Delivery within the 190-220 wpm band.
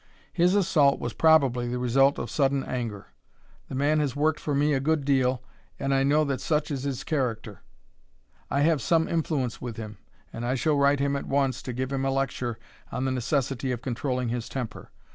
Yes: average, 200 wpm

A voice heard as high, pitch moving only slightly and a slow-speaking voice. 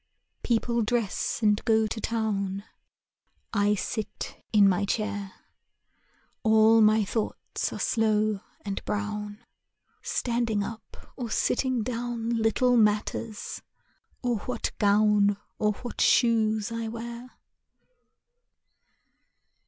Yes: high, 220 Hz; narrow, 2.0 semitones; slow, 100 wpm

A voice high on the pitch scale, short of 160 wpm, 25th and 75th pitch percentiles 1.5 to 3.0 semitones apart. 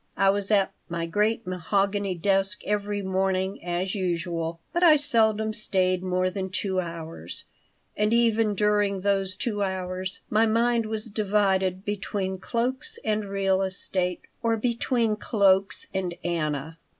Yes: high, 195 Hz; average, 140 wpm; narrow, 2.5 semitones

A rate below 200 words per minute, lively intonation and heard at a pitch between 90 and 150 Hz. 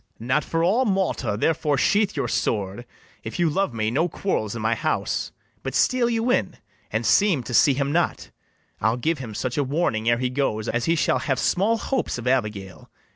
No: fast, 205 wpm; wide, 7.2 semitones; medium, 140 Hz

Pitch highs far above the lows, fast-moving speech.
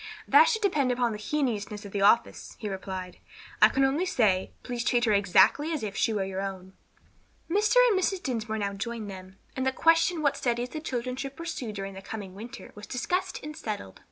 Yes: wide, 6.1 semitones; fast, 210 wpm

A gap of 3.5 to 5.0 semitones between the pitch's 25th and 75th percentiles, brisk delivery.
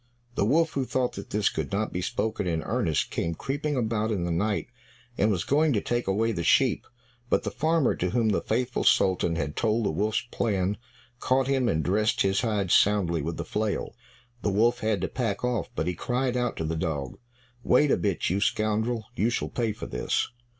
Yes: average, 4.6 semitones; fast, 210 wpm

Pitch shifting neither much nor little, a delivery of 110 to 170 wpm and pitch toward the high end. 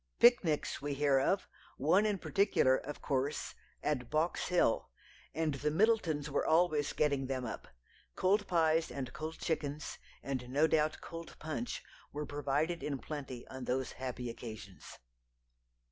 No: average, 3.4 semitones; average, 145 wpm; medium, 150 Hz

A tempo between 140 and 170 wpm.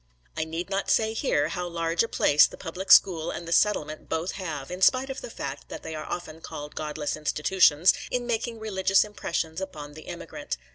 No: average, 200 wpm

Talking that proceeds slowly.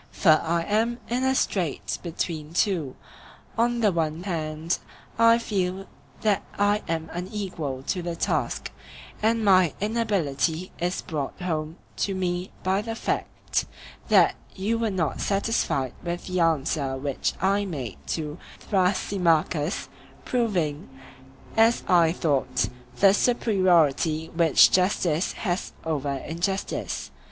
Yes: slow, 125 wpm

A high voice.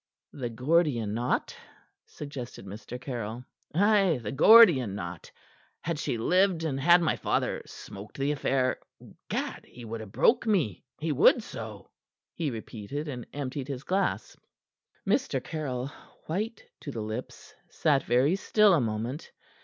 No: low, 135 Hz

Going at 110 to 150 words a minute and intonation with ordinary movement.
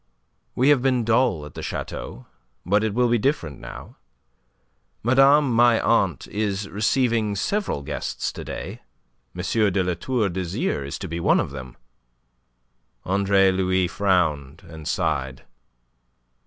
No: average, 140 wpm; wide, 6.0 semitones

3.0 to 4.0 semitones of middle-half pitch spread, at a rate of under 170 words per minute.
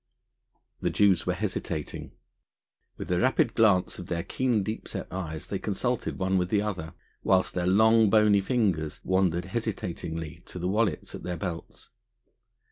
Yes: average, 3.4 semitones; average, 155 wpm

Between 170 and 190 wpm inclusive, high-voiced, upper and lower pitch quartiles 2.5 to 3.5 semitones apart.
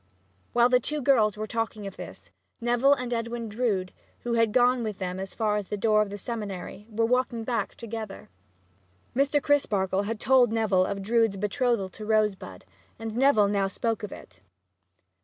Yes: average, 175 wpm; high, 225 Hz; average, 2.9 semitones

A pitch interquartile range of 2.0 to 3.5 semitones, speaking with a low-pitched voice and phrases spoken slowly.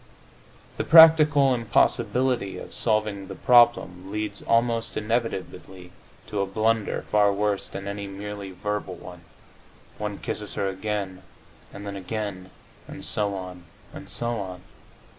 Yes: average, 2.9 semitones; low, 105 Hz; slow, 130 wpm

